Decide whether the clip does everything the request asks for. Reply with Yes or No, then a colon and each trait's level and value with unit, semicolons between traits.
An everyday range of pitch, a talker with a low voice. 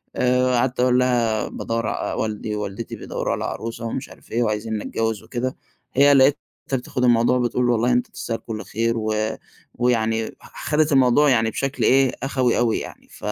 No: narrow, 2.1 semitones; low, 120 Hz